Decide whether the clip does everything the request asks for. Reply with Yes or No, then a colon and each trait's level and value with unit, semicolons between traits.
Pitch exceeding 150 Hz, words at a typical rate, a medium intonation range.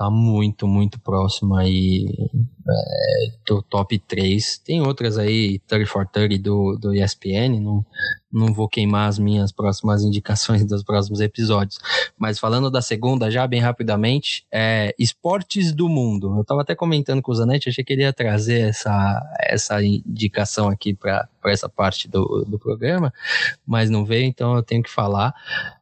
No: low, 110 Hz; average, 160 wpm; average, 3.0 semitones